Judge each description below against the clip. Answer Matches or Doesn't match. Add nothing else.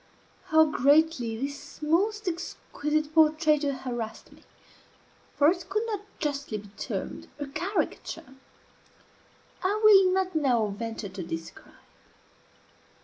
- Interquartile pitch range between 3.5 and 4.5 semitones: Doesn't match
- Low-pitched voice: Doesn't match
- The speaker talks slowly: Matches